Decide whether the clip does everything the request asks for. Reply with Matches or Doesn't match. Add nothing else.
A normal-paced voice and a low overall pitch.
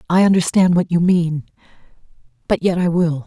Doesn't match